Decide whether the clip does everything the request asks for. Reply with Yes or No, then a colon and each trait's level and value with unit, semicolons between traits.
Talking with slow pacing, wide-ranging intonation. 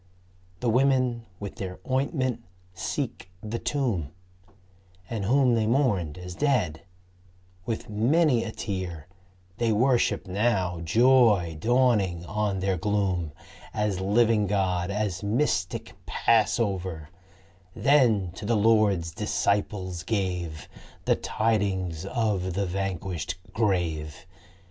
No: slow, 105 wpm; average, 4.3 semitones